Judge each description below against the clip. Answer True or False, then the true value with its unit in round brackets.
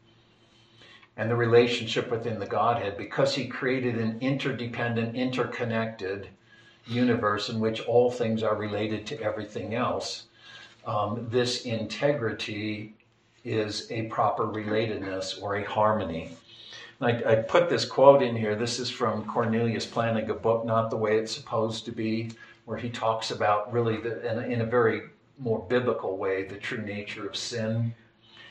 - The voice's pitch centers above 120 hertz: False (115 Hz)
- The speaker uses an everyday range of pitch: False (1.7 semitones)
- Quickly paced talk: False (155 wpm)